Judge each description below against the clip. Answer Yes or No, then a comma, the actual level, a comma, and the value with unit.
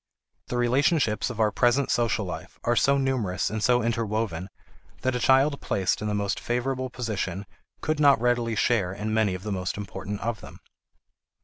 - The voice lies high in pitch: No, low, 115 Hz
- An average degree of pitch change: Yes, average, 3.4 semitones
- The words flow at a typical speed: Yes, average, 180 wpm